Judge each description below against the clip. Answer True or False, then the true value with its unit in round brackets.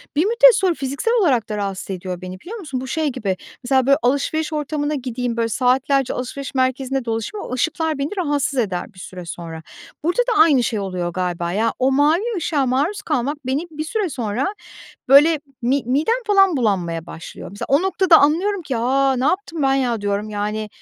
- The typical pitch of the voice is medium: False (270 Hz)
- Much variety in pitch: True (6.4 semitones)